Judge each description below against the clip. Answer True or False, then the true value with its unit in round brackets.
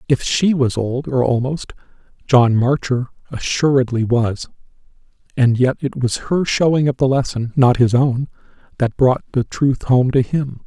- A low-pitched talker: True (130 Hz)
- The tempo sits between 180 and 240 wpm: False (165 wpm)